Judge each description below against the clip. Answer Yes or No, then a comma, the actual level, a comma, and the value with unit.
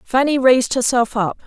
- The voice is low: No, very high, 250 Hz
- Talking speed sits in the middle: Yes, average, 165 wpm